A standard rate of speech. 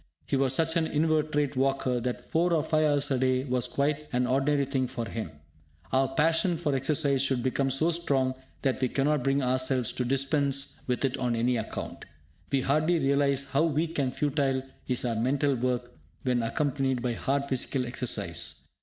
Yes: average, 180 wpm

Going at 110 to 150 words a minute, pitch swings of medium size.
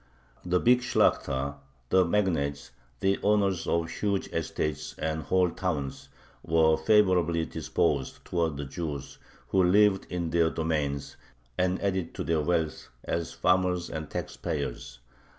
Yes: slow, 135 wpm; average, 3.3 semitones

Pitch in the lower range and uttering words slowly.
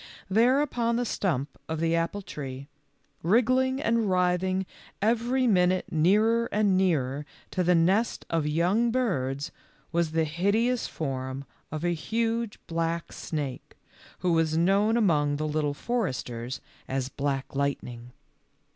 No: medium, 175 Hz; slow, 130 wpm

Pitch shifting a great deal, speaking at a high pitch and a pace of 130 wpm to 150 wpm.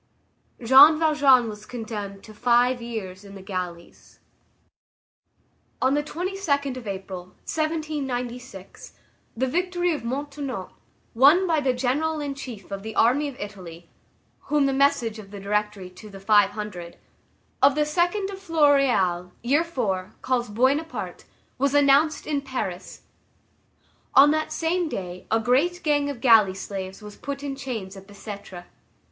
Yes: wide, 6.2 semitones; very high, 250 Hz; average, 145 wpm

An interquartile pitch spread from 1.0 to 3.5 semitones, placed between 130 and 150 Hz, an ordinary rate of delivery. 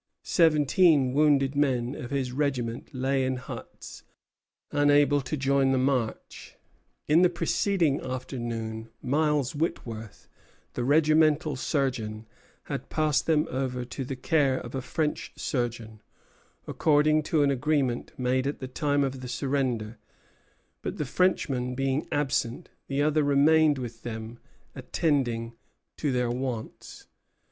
No: average, 3.1 semitones; low, 135 Hz; slow, 130 wpm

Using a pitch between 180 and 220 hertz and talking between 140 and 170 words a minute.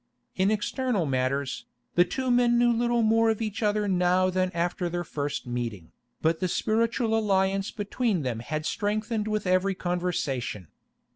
Yes: high, 190 Hz; average, 155 wpm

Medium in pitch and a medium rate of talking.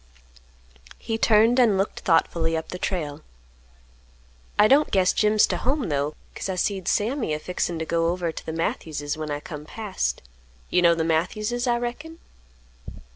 Yes: medium, 180 Hz; average, 170 wpm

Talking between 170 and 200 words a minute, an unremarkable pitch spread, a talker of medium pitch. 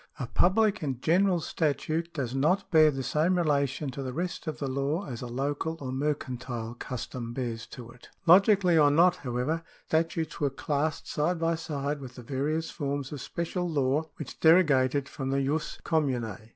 Yes: average, 180 wpm; average, 3.8 semitones; medium, 145 Hz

